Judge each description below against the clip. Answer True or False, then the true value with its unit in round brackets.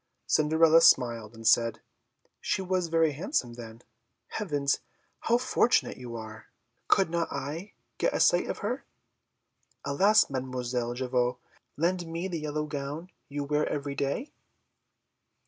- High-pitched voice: False (145 Hz)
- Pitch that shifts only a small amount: False (5.1 semitones)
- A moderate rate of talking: False (130 wpm)